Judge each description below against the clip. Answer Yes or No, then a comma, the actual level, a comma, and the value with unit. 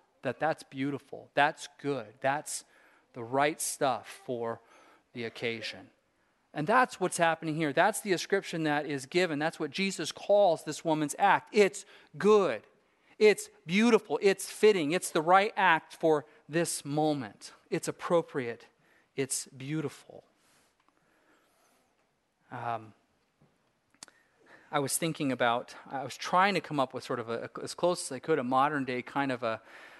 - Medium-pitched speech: Yes, medium, 150 Hz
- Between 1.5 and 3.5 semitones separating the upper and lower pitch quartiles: No, average, 4.8 semitones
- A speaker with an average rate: Yes, average, 145 wpm